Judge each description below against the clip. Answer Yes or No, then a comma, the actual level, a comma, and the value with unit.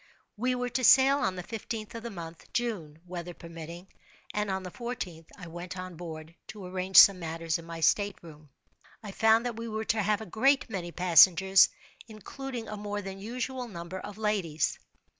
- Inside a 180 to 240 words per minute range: Yes, average, 190 wpm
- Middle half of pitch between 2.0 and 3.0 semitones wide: No, average, 4.5 semitones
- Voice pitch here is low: No, high, 195 Hz